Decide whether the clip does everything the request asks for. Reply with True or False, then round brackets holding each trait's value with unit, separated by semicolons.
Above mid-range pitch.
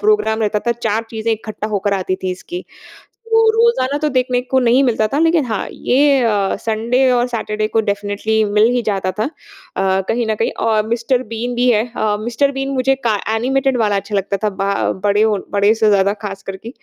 True (225 Hz)